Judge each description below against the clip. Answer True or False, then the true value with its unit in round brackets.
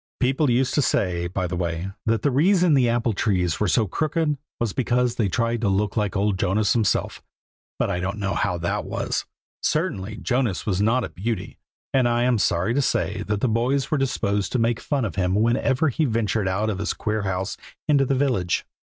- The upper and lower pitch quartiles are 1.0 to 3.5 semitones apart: False (4.7 semitones)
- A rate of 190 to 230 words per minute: True (205 wpm)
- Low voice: True (110 Hz)